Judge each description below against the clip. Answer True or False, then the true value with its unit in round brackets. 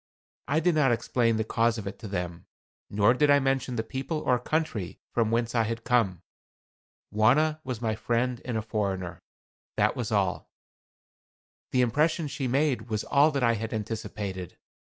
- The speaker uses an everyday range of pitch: True (3.6 semitones)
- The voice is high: False (115 Hz)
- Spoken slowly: False (175 wpm)